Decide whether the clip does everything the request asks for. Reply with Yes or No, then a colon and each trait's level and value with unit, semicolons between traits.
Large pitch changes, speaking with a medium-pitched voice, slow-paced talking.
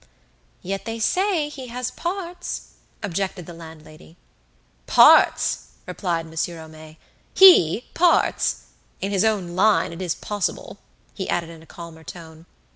Yes: wide, 6.0 semitones; medium, 180 Hz; slow, 130 wpm